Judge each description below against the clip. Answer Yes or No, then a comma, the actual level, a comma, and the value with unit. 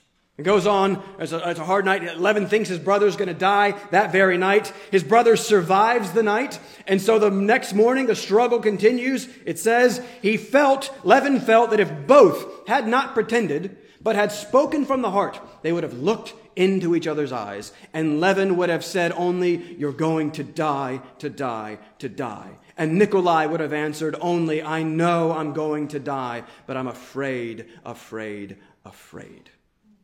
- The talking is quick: No, average, 180 wpm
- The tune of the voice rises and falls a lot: Yes, wide, 5.7 semitones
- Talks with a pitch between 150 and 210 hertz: Yes, medium, 185 Hz